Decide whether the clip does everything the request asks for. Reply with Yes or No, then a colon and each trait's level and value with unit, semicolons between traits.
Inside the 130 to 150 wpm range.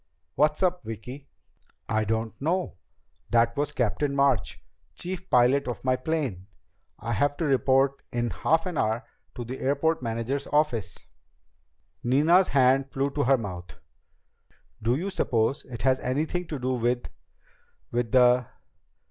Yes: average, 140 wpm